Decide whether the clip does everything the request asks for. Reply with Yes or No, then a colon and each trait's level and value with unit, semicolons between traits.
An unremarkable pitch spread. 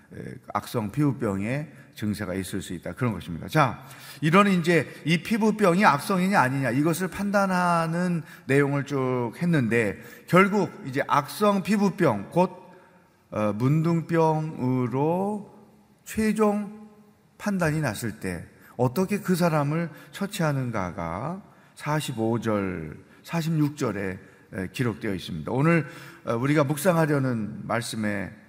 No: wide, 7.8 semitones